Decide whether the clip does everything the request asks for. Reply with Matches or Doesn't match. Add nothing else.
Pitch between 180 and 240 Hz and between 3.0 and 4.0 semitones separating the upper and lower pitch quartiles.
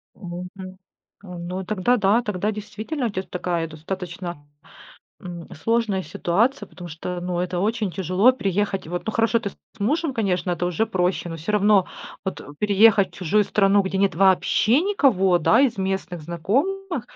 Matches